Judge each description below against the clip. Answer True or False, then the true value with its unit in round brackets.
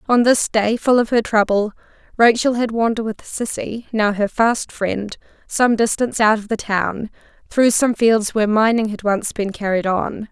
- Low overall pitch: False (220 Hz)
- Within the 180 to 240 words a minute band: True (185 wpm)